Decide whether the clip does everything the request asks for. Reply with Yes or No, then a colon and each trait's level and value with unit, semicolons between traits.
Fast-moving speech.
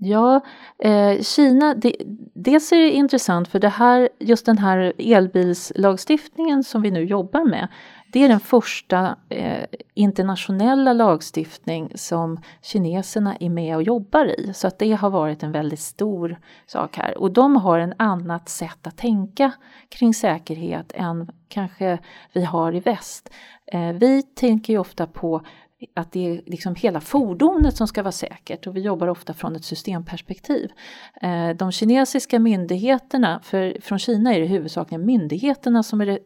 No: average, 155 wpm